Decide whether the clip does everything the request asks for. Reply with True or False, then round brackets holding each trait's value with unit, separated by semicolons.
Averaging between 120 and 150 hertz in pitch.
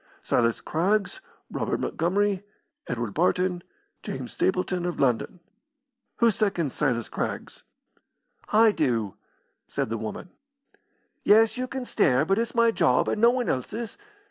False (185 Hz)